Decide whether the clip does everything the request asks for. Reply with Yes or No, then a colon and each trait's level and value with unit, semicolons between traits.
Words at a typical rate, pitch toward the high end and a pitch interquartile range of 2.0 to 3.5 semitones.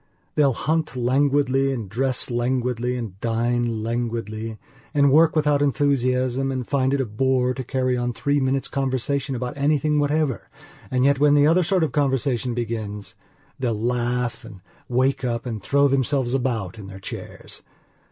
No: average, 160 wpm; low, 130 Hz; average, 2.9 semitones